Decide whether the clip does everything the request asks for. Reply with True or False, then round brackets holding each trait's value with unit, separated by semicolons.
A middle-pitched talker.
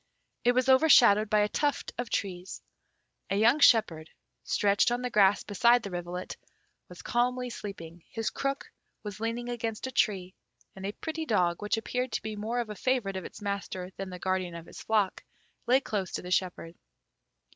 False (210 Hz)